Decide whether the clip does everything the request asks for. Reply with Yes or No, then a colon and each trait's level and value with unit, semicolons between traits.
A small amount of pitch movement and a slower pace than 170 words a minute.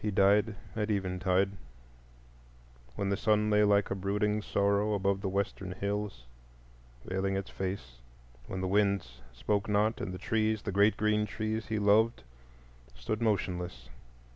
Yes: narrow, 1.8 semitones; average, 145 wpm